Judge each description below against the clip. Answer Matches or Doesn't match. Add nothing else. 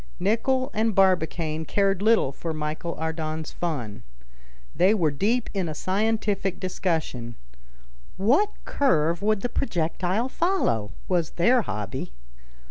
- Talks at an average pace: Doesn't match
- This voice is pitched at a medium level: Matches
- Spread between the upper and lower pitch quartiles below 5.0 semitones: Doesn't match